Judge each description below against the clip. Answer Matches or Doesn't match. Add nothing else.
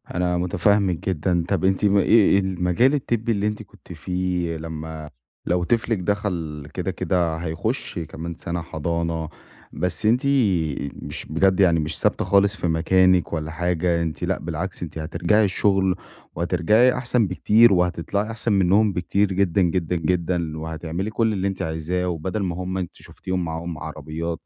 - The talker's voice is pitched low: Matches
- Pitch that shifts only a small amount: Doesn't match